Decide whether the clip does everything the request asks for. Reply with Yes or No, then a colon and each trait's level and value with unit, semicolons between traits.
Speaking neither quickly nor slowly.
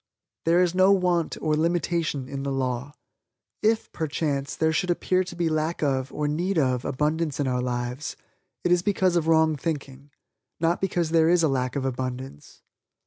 Yes: average, 180 wpm